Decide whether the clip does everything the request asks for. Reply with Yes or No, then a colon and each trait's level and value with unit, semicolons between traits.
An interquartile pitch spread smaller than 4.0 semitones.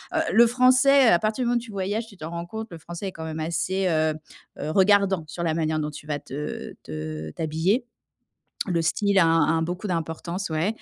No: average, 4.6 semitones